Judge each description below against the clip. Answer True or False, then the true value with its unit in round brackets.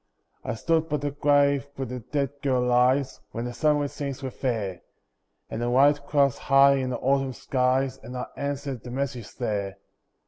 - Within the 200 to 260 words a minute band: False (180 wpm)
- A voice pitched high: False (135 Hz)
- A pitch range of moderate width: False (2.3 semitones)